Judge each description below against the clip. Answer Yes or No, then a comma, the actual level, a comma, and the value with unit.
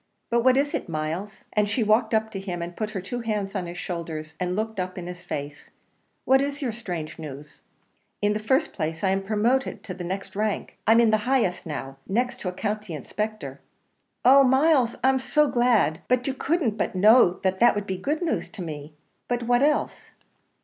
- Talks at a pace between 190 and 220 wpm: Yes, fast, 205 wpm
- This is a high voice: Yes, high, 210 Hz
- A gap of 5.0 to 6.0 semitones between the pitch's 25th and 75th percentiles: Yes, wide, 5.4 semitones